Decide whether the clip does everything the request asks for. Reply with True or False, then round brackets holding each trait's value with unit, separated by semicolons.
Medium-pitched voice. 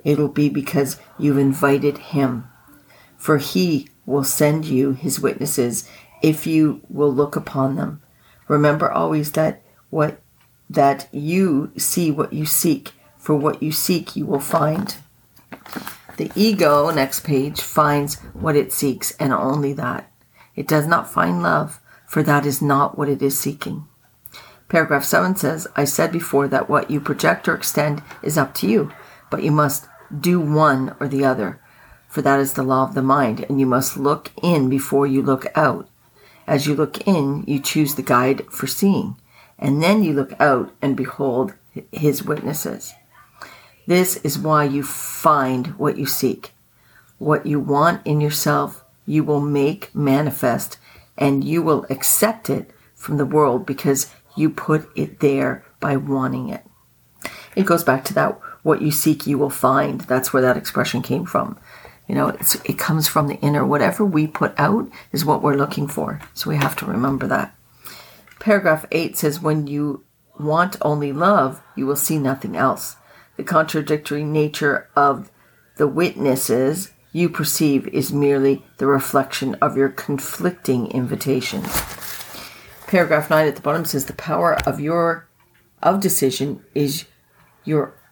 True (145 Hz)